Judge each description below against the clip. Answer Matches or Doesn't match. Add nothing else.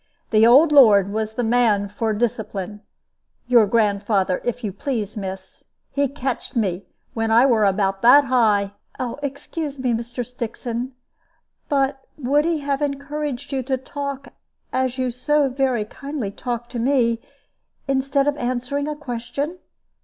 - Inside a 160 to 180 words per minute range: Doesn't match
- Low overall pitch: Doesn't match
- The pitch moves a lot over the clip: Doesn't match